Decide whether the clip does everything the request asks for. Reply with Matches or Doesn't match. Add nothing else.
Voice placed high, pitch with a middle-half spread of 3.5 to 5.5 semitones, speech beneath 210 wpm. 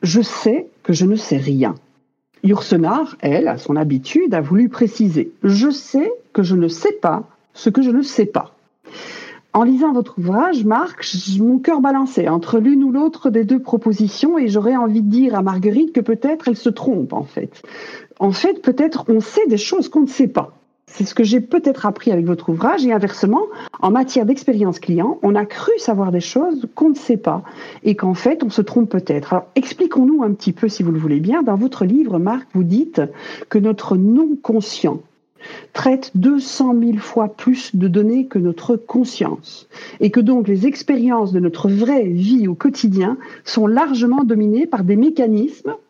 Matches